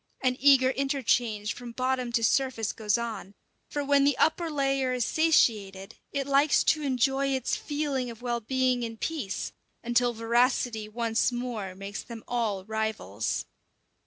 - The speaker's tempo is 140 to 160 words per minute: Yes, average, 150 wpm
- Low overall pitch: No, high, 245 Hz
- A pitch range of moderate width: Yes, average, 3.4 semitones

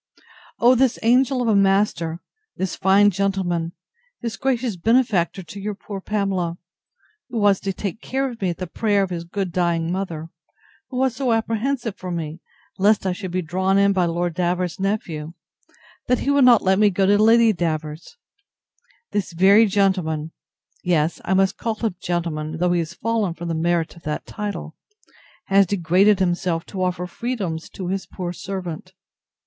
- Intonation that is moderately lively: Yes, average, 3.4 semitones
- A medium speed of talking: Yes, average, 175 wpm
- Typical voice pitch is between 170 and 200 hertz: Yes, high, 190 Hz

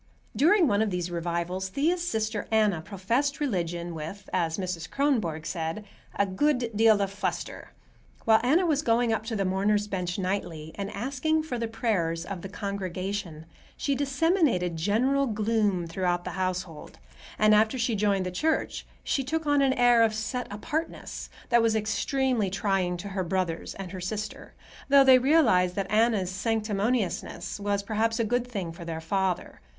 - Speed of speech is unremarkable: Yes, average, 165 wpm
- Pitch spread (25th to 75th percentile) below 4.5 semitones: No, average, 4.9 semitones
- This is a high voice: Yes, high, 205 Hz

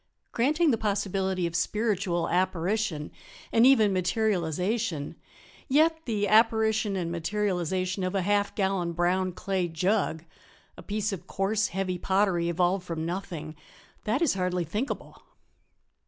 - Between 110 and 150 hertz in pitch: No, high, 190 Hz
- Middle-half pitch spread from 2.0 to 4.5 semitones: Yes, average, 3.4 semitones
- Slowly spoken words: Yes, slow, 125 wpm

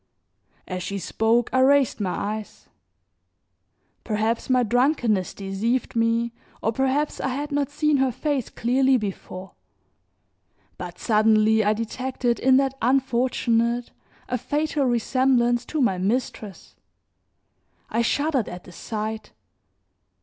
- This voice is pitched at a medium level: No, high, 240 Hz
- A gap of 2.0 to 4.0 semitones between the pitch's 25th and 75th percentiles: Yes, average, 3.4 semitones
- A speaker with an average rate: No, slow, 120 wpm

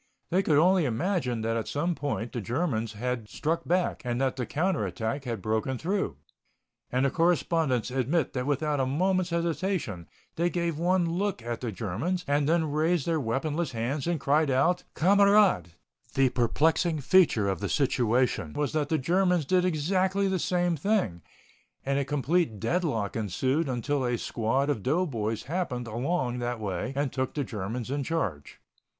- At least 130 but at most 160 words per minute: No, average, 170 wpm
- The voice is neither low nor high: Yes, medium, 145 Hz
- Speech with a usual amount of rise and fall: No, wide, 6.2 semitones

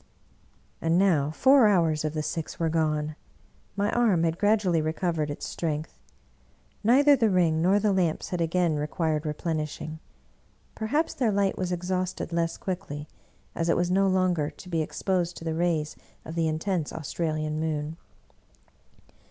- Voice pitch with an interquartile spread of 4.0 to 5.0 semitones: No, average, 3.2 semitones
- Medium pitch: Yes, medium, 170 Hz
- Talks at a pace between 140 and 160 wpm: Yes, average, 155 wpm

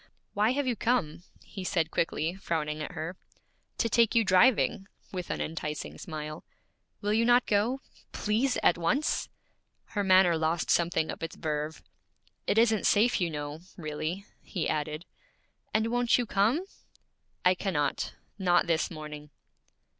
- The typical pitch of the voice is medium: Yes, medium, 180 Hz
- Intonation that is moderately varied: No, wide, 5.9 semitones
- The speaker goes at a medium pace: Yes, average, 145 wpm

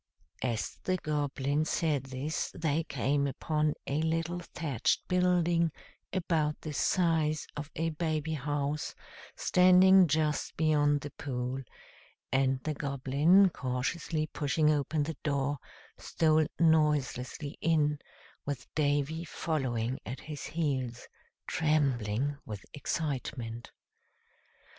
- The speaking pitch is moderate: Yes, medium, 150 Hz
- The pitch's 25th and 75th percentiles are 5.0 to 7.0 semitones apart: No, narrow, 2.6 semitones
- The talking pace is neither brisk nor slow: No, slow, 105 wpm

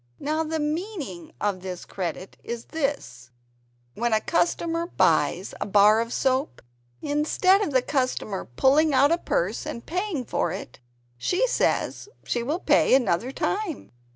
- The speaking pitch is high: Yes, very high, 270 Hz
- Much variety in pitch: Yes, wide, 7.2 semitones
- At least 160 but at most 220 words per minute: No, average, 145 wpm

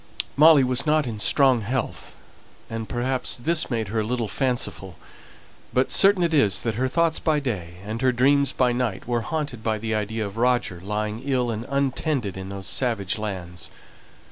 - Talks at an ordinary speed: Yes, average, 180 wpm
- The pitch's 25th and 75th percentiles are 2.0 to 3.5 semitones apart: No, average, 4.1 semitones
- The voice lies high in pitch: No, low, 120 Hz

